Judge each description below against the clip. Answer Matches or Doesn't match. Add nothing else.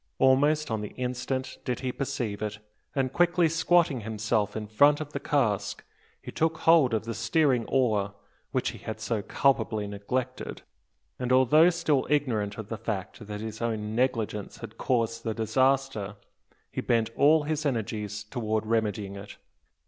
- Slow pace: Doesn't match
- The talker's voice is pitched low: Matches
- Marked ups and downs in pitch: Doesn't match